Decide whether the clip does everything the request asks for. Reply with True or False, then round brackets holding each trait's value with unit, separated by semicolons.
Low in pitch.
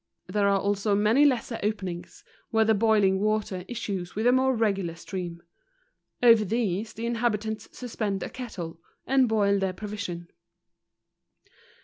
False (210 Hz)